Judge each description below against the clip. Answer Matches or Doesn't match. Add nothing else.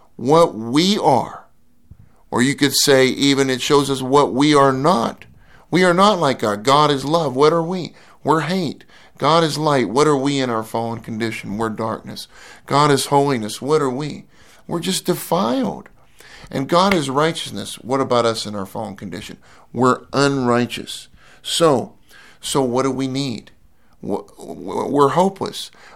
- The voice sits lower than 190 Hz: Matches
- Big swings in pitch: Doesn't match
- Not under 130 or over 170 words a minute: Matches